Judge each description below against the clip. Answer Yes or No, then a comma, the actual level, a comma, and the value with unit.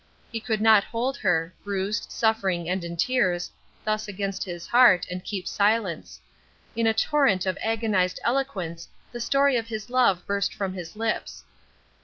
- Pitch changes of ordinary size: Yes, average, 3.9 semitones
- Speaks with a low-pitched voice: No, high, 205 Hz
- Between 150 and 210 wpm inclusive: Yes, average, 160 wpm